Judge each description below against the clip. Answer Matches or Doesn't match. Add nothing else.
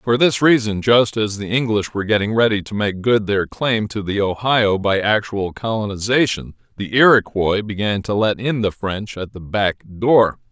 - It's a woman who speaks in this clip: Doesn't match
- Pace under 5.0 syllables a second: Matches